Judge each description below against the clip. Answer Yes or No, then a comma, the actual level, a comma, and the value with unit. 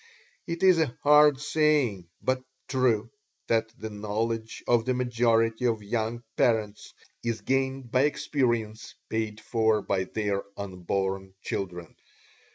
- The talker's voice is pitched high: No, low, 115 Hz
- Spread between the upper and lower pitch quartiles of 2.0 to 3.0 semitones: No, average, 3.5 semitones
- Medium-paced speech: No, slow, 125 wpm